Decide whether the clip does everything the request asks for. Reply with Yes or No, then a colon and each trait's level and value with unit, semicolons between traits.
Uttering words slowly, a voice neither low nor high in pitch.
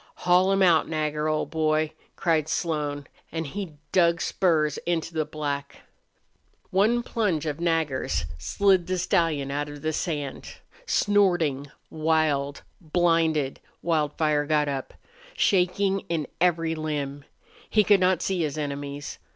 Yes: slow, 130 wpm; medium, 155 Hz